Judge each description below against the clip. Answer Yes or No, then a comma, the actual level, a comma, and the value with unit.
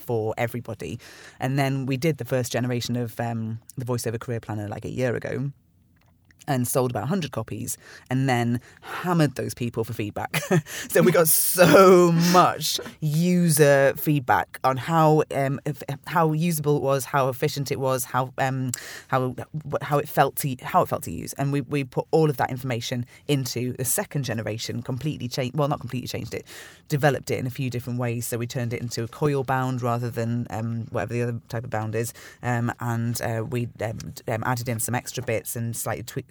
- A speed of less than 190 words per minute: No, average, 200 wpm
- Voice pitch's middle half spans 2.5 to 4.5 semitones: Yes, average, 3.2 semitones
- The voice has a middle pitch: No, low, 130 Hz